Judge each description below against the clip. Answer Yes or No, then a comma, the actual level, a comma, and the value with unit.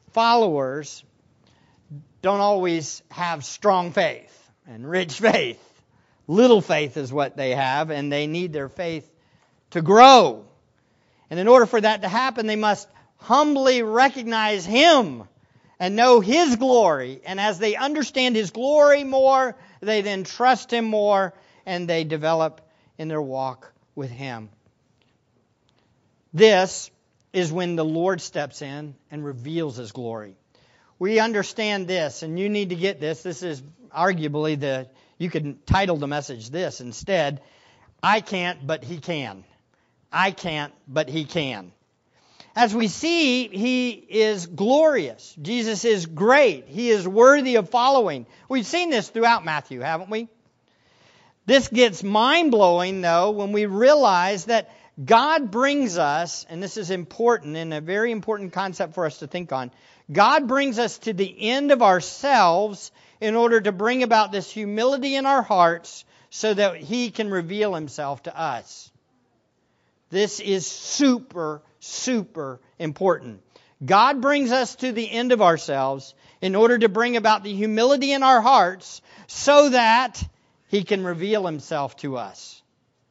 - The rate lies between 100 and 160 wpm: Yes, average, 145 wpm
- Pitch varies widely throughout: Yes, wide, 7.2 semitones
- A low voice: No, high, 190 Hz